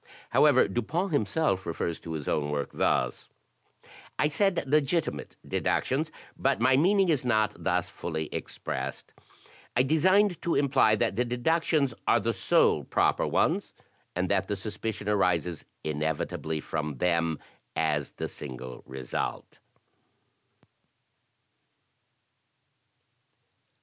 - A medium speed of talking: No, slow, 115 wpm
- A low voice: Yes, low, 110 Hz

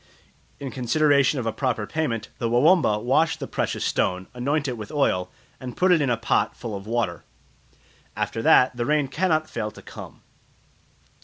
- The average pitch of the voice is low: Yes, low, 125 Hz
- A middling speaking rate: Yes, average, 175 wpm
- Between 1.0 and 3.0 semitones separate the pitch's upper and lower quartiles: No, average, 4.8 semitones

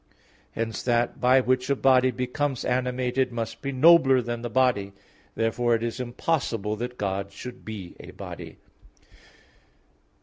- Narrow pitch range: Yes, narrow, 2.2 semitones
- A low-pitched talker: Yes, low, 125 Hz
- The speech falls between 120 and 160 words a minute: Yes, average, 140 wpm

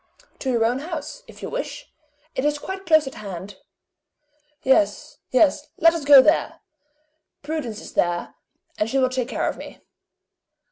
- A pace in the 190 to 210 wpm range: No, average, 160 wpm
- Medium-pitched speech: No, very high, 270 Hz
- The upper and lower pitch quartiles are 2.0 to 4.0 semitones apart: No, average, 5.1 semitones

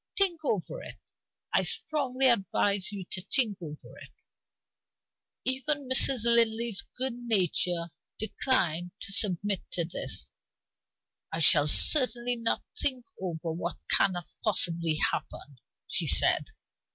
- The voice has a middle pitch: No, high, 205 Hz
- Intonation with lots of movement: Yes, wide, 6.5 semitones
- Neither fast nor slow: No, slow, 115 wpm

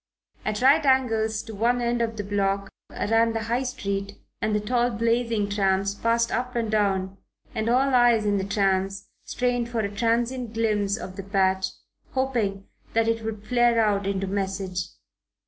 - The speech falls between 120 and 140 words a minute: No, average, 170 wpm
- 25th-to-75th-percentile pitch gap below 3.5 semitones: Yes, average, 3.1 semitones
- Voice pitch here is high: Yes, high, 220 Hz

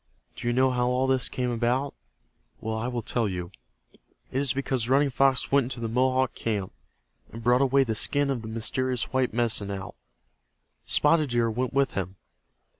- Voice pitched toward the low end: Yes, low, 125 Hz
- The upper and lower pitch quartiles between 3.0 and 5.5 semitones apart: No, narrow, 2.5 semitones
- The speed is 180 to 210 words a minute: Yes, average, 185 wpm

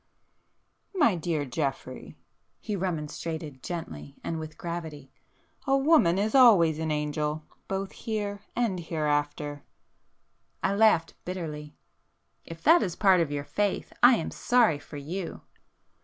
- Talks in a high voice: No, medium, 165 Hz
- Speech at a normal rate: No, slow, 120 wpm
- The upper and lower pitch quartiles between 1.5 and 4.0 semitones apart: No, average, 5.1 semitones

